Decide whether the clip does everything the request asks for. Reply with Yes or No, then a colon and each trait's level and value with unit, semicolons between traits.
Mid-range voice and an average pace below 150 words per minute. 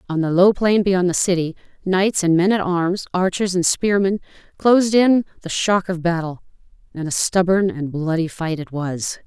No: medium, 180 Hz; average, 190 wpm